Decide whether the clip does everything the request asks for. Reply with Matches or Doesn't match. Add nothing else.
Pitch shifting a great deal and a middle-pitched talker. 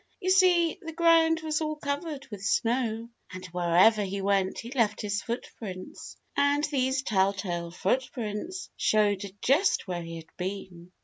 Doesn't match